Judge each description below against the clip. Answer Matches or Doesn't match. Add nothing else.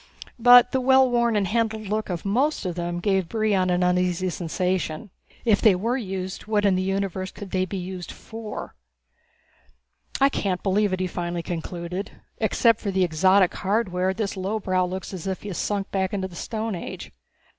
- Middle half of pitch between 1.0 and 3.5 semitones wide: Matches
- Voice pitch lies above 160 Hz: Matches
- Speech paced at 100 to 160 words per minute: Doesn't match